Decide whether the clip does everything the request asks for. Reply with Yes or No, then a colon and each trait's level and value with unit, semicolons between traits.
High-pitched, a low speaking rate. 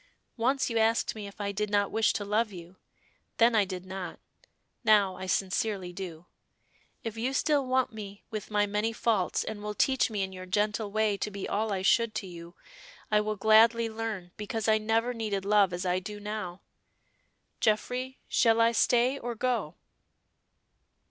No: high, 210 Hz; average, 180 wpm